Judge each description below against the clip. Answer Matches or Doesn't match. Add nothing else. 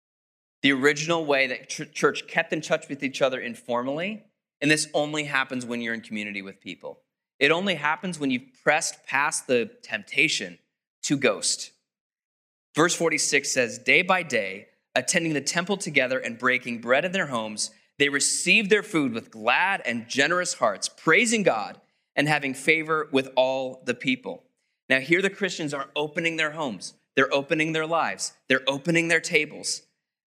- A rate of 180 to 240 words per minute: Doesn't match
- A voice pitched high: Doesn't match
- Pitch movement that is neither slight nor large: Matches